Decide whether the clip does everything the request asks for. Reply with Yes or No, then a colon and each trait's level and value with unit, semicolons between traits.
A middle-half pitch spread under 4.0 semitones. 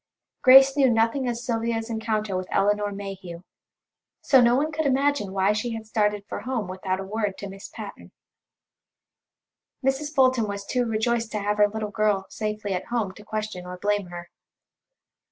Yes: average, 3.2 semitones